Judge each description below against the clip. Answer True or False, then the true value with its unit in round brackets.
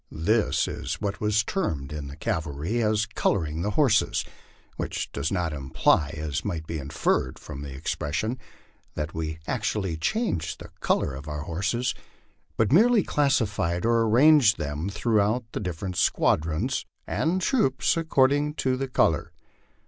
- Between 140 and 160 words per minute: True (150 wpm)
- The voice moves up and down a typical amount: False (8.1 semitones)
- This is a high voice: False (100 Hz)